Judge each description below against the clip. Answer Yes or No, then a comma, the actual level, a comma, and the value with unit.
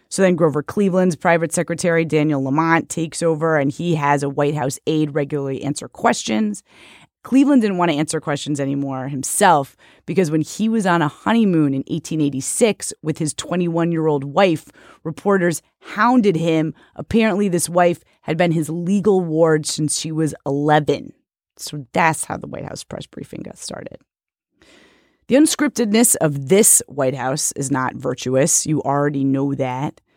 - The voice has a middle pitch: Yes, medium, 155 Hz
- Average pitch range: Yes, average, 3.6 semitones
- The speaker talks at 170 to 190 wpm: No, average, 160 wpm